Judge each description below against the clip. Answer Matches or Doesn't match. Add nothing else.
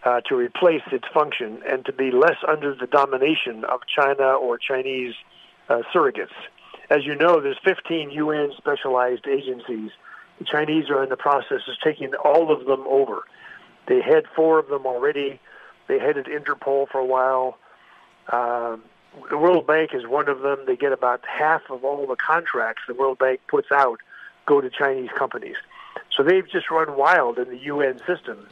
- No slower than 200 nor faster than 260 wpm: Doesn't match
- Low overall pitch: Doesn't match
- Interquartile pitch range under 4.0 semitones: Doesn't match